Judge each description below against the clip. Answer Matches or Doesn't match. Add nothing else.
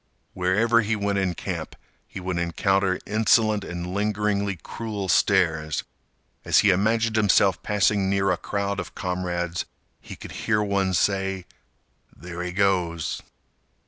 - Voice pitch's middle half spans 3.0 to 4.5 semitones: Doesn't match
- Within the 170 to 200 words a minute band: Doesn't match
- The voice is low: Matches